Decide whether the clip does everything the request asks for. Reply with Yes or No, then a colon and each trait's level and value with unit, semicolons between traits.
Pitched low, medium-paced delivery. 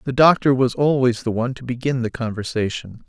Yes: low, 125 Hz; average, 195 wpm